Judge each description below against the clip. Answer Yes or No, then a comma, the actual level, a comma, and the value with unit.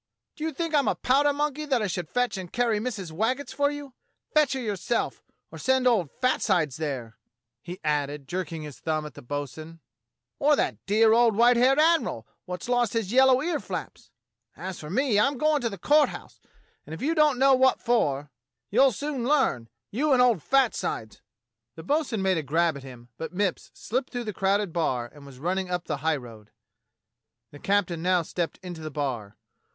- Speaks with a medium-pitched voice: No, high, 205 Hz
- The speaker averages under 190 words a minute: No, average, 200 wpm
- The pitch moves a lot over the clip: Yes, wide, 8.8 semitones